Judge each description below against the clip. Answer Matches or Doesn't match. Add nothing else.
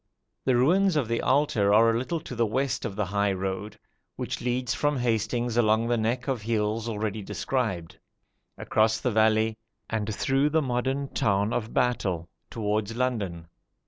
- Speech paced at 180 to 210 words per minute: Doesn't match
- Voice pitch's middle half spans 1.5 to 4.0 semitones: Matches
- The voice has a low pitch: Matches